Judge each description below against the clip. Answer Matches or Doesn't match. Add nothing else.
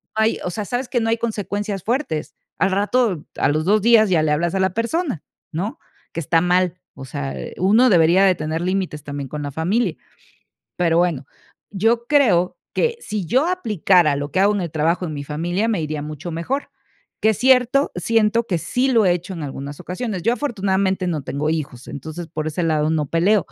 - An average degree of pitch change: Doesn't match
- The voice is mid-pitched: Matches